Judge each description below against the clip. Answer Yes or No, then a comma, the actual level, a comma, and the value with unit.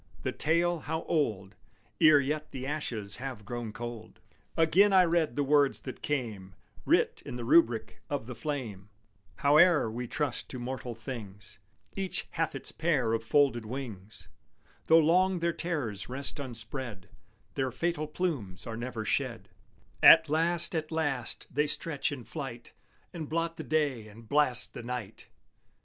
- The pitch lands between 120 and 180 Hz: Yes, low, 135 Hz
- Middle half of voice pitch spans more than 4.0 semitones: Yes, wide, 5.5 semitones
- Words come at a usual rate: Yes, average, 155 wpm